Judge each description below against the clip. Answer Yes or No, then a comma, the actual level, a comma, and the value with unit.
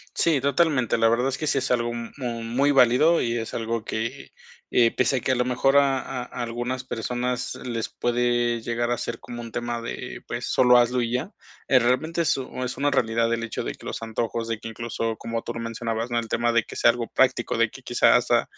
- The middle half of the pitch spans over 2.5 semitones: No, narrow, 1.6 semitones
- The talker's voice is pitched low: Yes, low, 120 Hz